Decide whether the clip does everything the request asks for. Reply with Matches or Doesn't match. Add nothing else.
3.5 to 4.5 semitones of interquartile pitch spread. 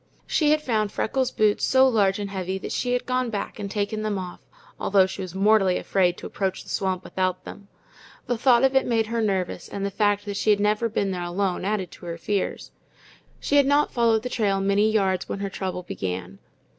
Doesn't match